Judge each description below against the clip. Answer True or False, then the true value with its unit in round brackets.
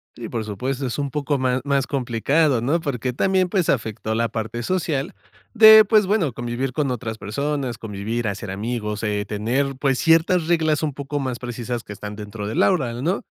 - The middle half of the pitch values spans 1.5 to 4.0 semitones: False (4.8 semitones)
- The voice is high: False (130 Hz)